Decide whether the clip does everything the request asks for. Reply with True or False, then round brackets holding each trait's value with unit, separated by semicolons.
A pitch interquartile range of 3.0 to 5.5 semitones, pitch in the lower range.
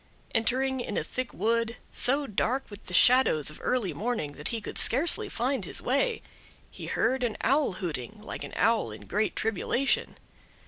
False (4.0 semitones; 235 Hz)